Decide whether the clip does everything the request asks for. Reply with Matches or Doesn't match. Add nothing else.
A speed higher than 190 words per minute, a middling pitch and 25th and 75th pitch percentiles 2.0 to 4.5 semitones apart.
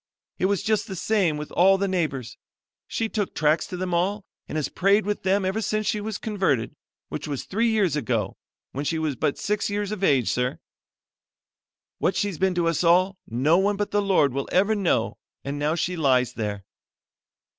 Doesn't match